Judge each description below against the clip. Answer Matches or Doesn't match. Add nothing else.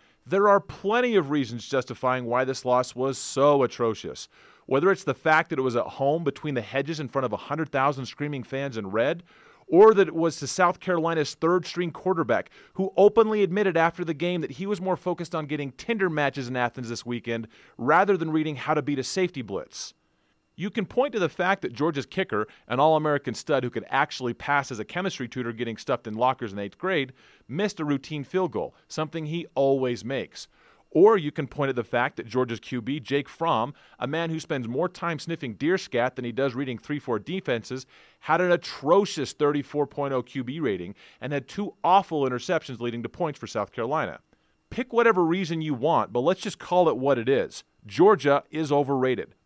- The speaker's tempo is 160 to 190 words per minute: Doesn't match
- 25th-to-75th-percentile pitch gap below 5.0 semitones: Doesn't match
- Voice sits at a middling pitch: Matches